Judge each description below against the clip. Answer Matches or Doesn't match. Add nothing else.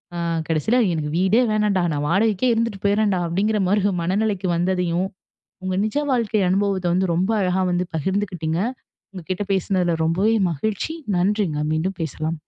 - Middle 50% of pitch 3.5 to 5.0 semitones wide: Doesn't match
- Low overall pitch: Doesn't match